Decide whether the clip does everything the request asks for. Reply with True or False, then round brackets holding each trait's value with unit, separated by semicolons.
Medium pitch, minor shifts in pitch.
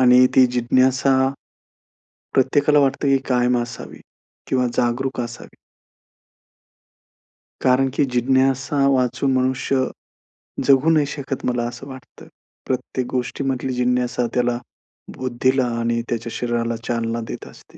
False (130 Hz; 1.6 semitones)